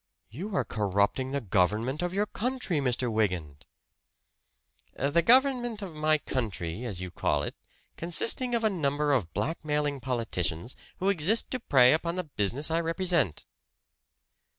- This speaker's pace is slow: No, average, 145 wpm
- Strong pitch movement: Yes, wide, 8.4 semitones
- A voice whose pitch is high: No, medium, 145 Hz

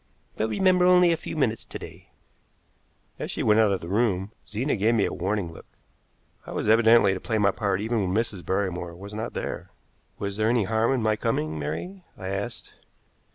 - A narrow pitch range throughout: No, average, 3.3 semitones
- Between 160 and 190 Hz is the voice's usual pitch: No, low, 110 Hz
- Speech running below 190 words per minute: No, average, 200 wpm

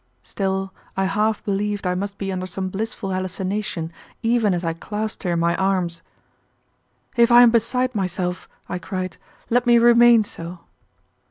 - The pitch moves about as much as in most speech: Yes, average, 3.3 semitones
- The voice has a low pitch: No, high, 195 Hz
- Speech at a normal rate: Yes, average, 160 wpm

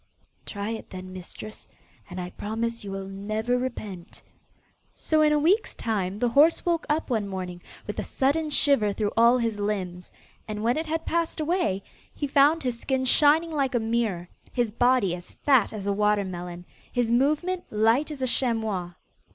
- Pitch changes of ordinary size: No, wide, 5.9 semitones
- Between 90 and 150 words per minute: No, average, 180 wpm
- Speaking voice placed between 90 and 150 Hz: No, high, 230 Hz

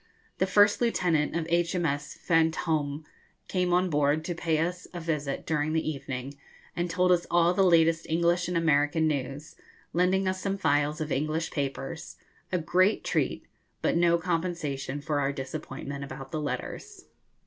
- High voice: No, medium, 160 Hz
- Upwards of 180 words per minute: No, average, 160 wpm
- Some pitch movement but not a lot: Yes, average, 3.2 semitones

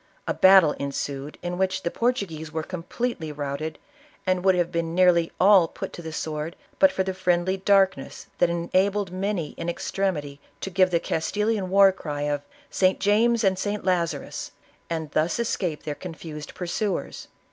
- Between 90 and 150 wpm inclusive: No, average, 170 wpm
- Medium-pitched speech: Yes, medium, 180 Hz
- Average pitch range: Yes, average, 3.3 semitones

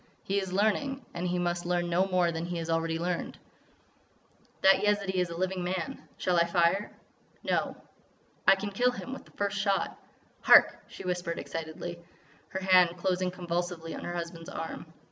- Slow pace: No, average, 175 wpm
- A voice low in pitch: No, medium, 180 Hz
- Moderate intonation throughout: No, narrow, 2.0 semitones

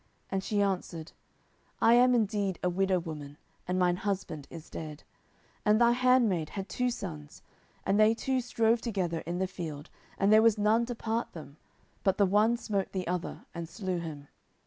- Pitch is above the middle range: Yes, high, 195 Hz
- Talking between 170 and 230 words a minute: Yes, average, 185 wpm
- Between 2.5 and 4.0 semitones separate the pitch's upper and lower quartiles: No, average, 4.6 semitones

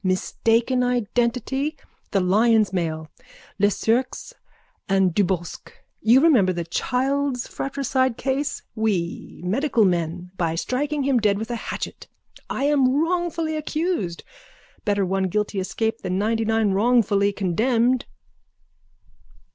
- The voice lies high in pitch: Yes, high, 225 Hz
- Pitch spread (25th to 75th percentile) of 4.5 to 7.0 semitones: Yes, wide, 5.4 semitones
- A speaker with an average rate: No, slow, 110 wpm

